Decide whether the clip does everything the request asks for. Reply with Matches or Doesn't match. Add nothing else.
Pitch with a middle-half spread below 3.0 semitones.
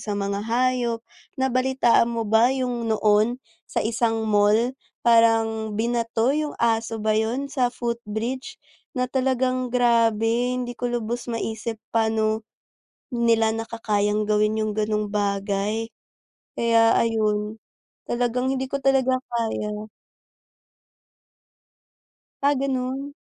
Matches